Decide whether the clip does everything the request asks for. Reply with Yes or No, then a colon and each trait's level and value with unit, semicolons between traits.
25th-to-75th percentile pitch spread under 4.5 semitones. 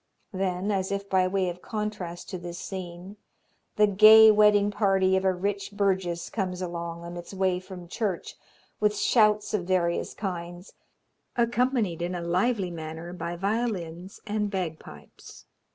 Yes: average, 3.0 semitones